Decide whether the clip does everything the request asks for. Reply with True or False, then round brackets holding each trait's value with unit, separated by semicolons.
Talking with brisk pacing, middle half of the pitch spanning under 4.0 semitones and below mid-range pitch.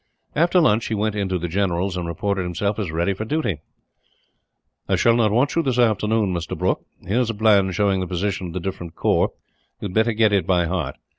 True (220 wpm; 3.5 semitones; 100 Hz)